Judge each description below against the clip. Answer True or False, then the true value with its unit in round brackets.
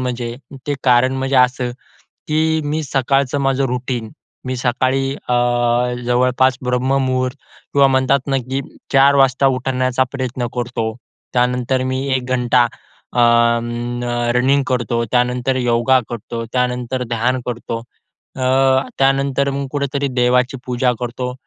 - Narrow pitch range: True (1.6 semitones)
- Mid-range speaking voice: False (130 Hz)